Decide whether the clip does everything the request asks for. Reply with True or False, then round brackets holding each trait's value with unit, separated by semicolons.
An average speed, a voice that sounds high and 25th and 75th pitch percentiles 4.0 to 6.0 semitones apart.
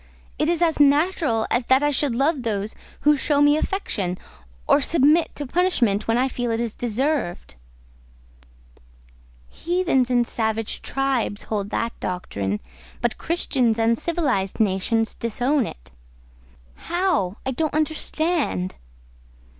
False (130 wpm; 255 Hz; 5.5 semitones)